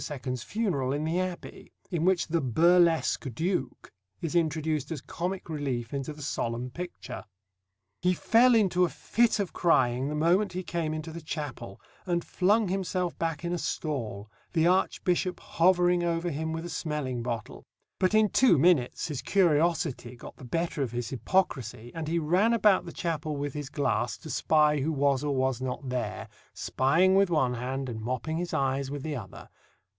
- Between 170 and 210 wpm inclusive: Yes, average, 180 wpm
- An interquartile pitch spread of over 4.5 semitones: Yes, average, 5.0 semitones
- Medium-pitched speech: Yes, medium, 155 Hz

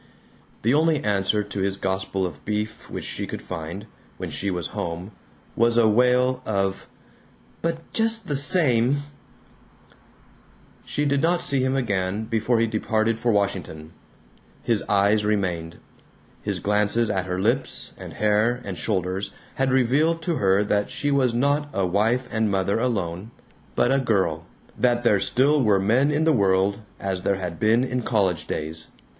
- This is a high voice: No, low, 110 Hz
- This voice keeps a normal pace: Yes, average, 160 wpm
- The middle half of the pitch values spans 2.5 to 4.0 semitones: No, average, 4.7 semitones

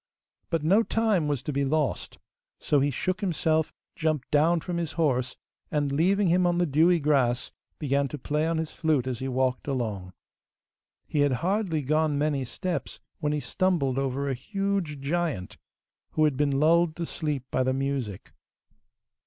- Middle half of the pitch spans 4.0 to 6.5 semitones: No, average, 3.6 semitones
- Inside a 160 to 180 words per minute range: Yes, average, 170 wpm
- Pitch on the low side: No, medium, 150 Hz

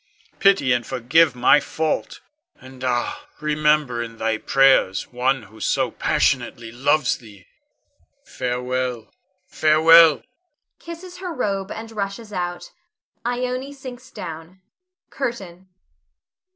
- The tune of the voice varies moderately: No, wide, 8.1 semitones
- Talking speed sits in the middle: No, slow, 105 wpm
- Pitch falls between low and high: Yes, medium, 155 Hz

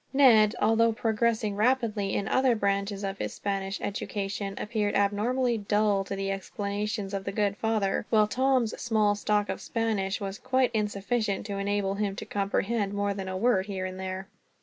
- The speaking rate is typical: Yes, average, 170 wpm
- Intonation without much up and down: Yes, narrow, 2.1 semitones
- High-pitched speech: Yes, high, 205 Hz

